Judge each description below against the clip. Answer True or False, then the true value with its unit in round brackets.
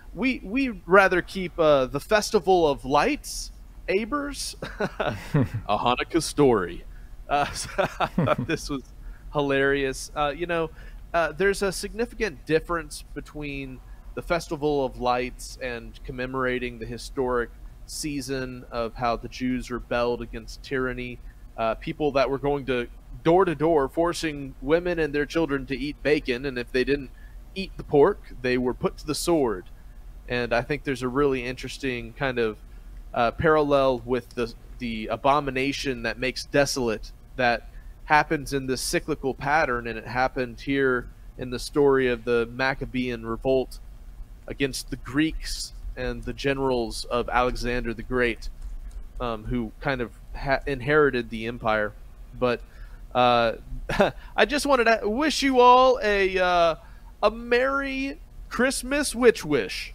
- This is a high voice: False (135 Hz)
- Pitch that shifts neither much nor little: True (4.6 semitones)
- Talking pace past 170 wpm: False (145 wpm)